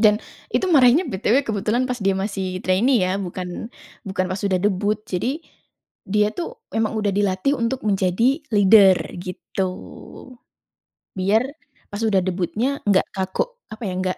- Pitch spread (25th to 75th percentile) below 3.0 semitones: No, average, 3.7 semitones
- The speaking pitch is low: No, high, 205 Hz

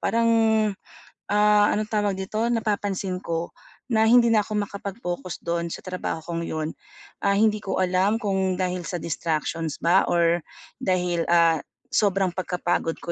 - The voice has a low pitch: No, high, 190 Hz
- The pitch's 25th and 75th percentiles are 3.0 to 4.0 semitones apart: Yes, average, 3.4 semitones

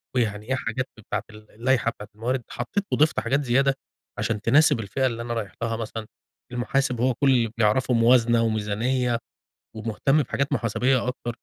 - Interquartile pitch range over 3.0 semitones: No, average, 2.7 semitones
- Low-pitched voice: Yes, low, 120 Hz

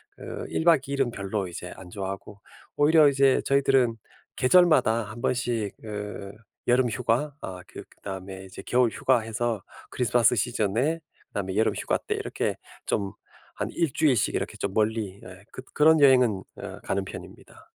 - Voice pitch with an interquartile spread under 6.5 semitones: Yes, average, 5.1 semitones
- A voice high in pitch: No, low, 115 Hz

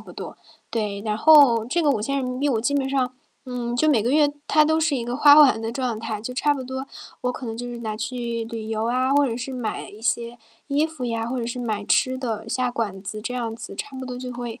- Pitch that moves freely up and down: No, average, 2.8 semitones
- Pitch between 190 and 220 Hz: No, high, 245 Hz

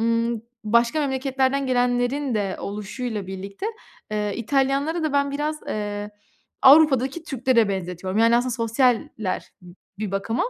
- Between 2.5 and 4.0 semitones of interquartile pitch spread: No, average, 4.4 semitones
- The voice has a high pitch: Yes, high, 240 Hz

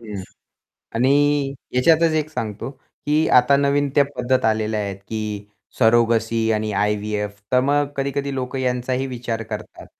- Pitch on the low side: Yes, low, 125 Hz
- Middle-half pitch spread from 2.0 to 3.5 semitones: No, average, 4.3 semitones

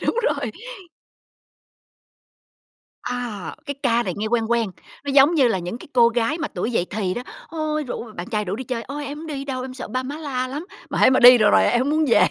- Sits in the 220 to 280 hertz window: Yes, very high, 250 Hz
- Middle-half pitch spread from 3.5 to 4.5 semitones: Yes, average, 3.8 semitones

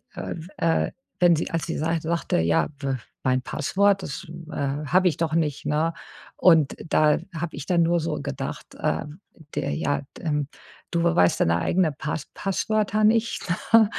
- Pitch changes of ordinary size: Yes, average, 3.7 semitones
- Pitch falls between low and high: Yes, medium, 160 Hz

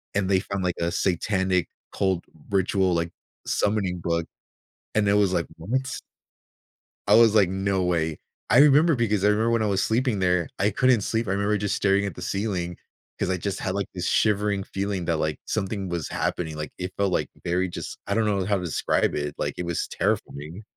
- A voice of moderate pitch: No, very low, 95 Hz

